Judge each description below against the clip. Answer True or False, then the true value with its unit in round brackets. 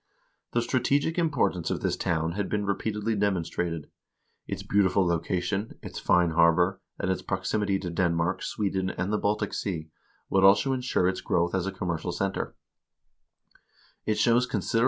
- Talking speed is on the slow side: False (145 wpm)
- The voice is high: False (95 Hz)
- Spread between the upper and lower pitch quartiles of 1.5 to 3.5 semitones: True (3.0 semitones)